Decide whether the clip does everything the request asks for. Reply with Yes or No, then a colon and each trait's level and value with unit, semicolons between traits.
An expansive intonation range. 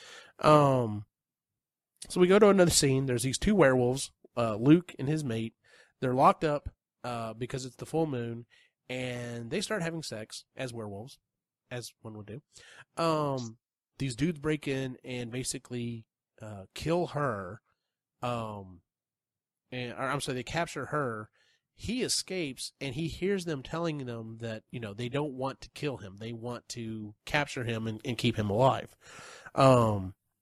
No: average, 4.4 semitones